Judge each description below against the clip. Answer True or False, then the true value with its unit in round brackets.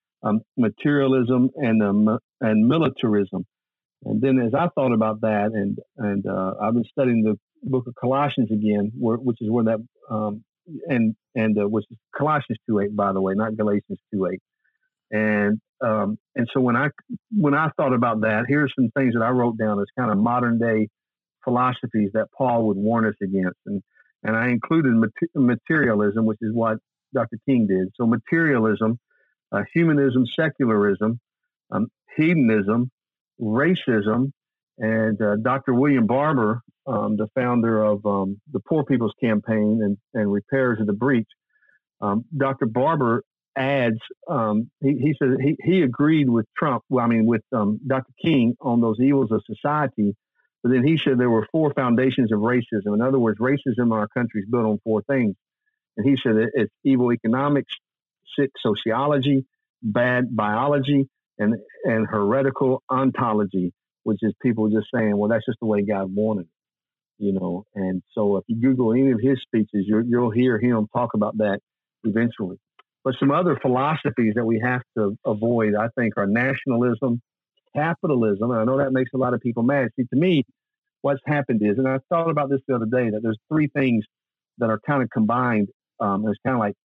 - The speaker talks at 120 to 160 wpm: False (180 wpm)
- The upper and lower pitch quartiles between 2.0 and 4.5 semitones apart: True (3.7 semitones)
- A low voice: True (120 Hz)